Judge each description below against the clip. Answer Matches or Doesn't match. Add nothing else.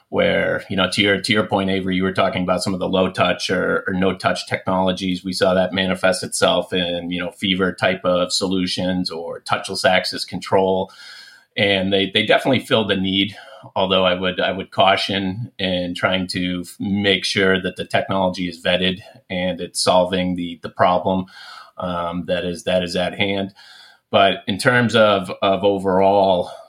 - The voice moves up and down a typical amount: Doesn't match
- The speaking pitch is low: Matches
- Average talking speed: Matches